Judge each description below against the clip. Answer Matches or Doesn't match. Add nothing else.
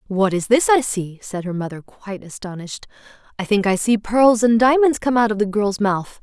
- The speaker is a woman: Matches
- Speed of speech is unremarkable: Doesn't match